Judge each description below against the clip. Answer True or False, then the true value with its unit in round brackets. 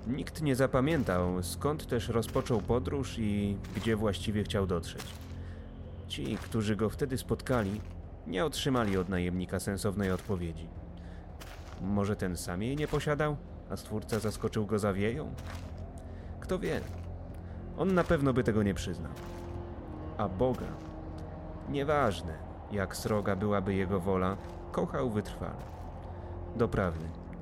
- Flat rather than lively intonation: False (3.8 semitones)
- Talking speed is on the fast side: False (120 wpm)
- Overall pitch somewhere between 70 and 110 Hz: True (95 Hz)